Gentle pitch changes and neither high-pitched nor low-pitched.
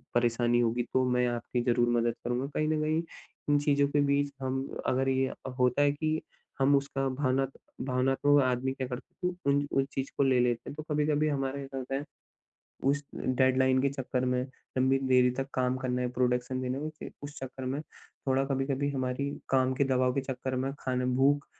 No: narrow, 1.8 semitones; low, 130 Hz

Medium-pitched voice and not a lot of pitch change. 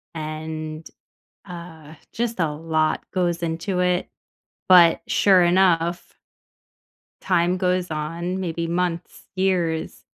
Yes: medium, 170 Hz; narrow, 2.1 semitones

